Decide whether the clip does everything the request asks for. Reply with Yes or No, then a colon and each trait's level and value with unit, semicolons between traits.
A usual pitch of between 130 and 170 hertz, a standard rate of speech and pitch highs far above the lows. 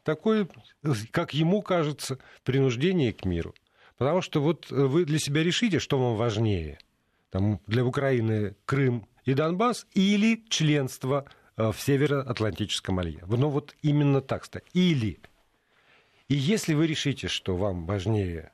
Yes: low, 135 Hz; average, 130 wpm; wide, 6.6 semitones